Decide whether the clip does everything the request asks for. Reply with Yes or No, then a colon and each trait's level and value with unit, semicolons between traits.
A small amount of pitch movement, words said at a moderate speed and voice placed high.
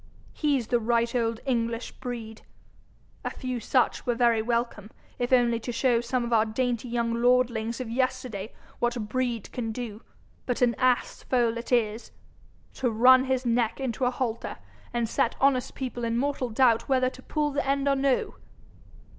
Yes: narrow, 1.8 semitones; average, 170 wpm; high, 240 Hz